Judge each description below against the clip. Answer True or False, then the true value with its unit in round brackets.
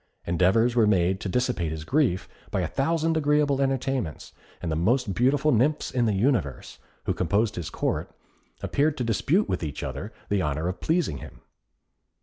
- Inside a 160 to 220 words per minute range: True (170 wpm)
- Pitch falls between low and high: False (115 Hz)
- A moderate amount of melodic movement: False (7.6 semitones)